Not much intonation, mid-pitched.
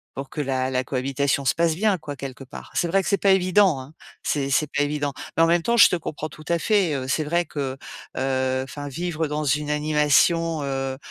No: average, 3.6 semitones; medium, 150 Hz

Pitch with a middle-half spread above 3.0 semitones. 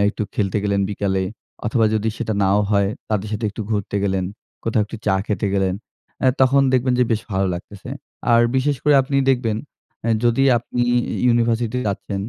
Yes: average, 3.4 semitones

